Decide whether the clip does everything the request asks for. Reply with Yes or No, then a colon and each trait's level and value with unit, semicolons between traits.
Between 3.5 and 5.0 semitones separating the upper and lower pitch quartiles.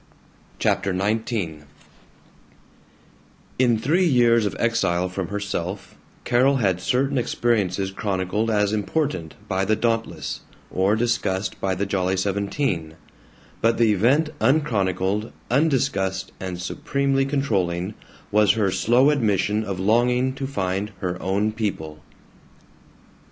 Yes: average, 4.3 semitones